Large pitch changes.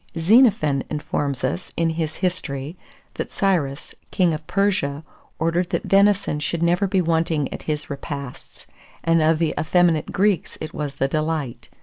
No: average, 3.4 semitones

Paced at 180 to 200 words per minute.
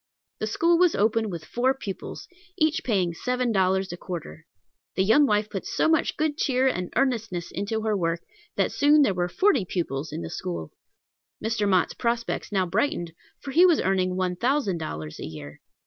Yes: average, 185 wpm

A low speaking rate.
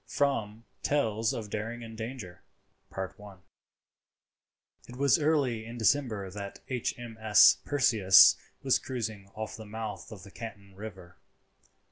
Yes: slow, 120 wpm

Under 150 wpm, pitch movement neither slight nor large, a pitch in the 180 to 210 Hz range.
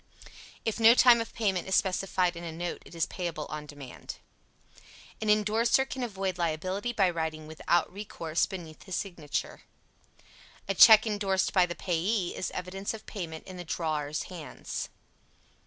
No: average, 155 wpm; average, 4.0 semitones; medium, 185 Hz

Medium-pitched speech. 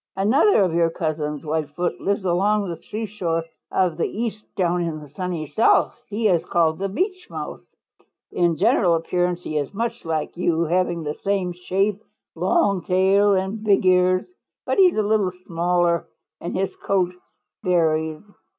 Yes: medium, 180 Hz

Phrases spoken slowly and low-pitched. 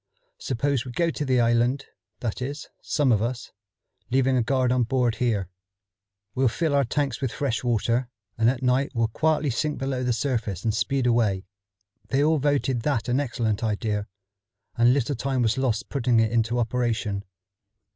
No: average, 175 wpm; low, 125 Hz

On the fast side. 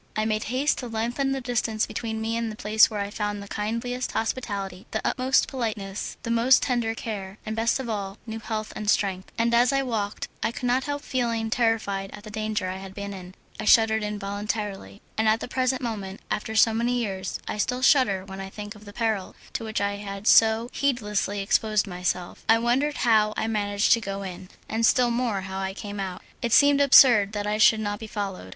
Yes: fast, 220 wpm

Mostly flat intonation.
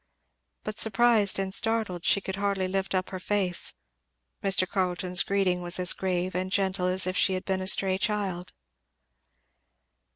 Yes: narrow, 1.5 semitones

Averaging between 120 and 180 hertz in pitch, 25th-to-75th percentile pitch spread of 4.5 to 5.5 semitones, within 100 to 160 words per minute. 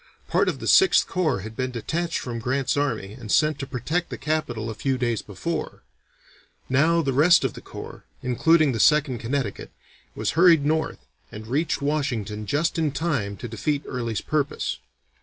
No: low, 135 Hz; average, 5.0 semitones; average, 175 wpm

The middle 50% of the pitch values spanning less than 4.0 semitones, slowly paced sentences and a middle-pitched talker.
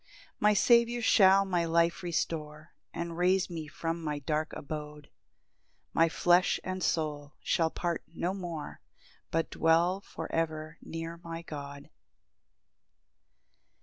Yes: narrow, 2.4 semitones; slow, 125 wpm; medium, 165 Hz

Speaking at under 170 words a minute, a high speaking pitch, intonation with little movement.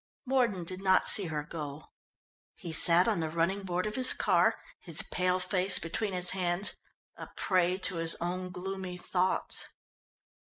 No: average, 160 wpm; medium, 180 Hz; narrow, 2.1 semitones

